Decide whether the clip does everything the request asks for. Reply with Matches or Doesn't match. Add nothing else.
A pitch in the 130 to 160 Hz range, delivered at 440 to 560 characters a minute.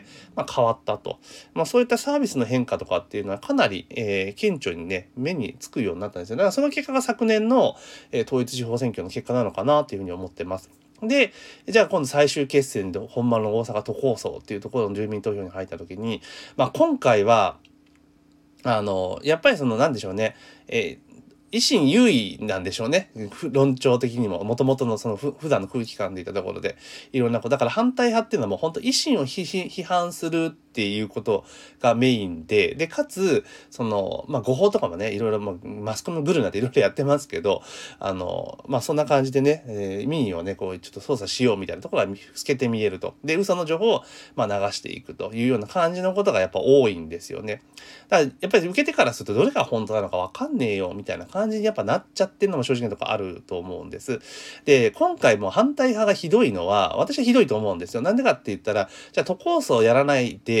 Matches